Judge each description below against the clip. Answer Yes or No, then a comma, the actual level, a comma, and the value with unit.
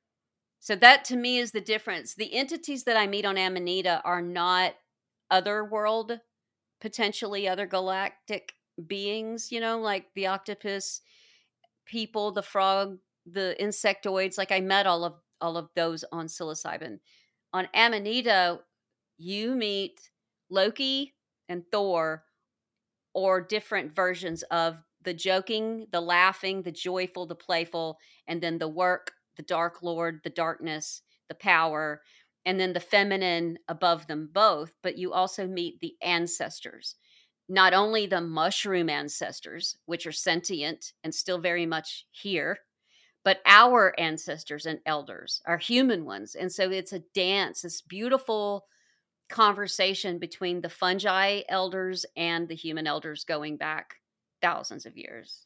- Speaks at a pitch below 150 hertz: No, medium, 185 Hz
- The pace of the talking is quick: No, slow, 135 wpm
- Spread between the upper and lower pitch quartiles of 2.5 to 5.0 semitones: Yes, average, 3.3 semitones